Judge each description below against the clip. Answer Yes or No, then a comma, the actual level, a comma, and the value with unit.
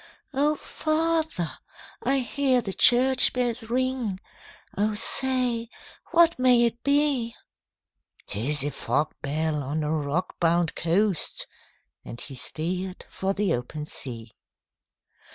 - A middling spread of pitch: No, wide, 8.7 semitones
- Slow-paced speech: Yes, slow, 115 wpm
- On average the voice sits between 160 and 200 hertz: No, high, 210 Hz